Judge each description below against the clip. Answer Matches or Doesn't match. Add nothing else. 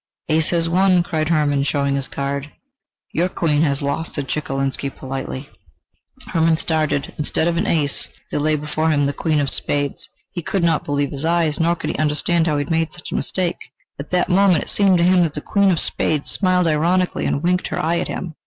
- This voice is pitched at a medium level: Matches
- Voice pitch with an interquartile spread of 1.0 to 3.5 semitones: Matches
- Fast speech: Matches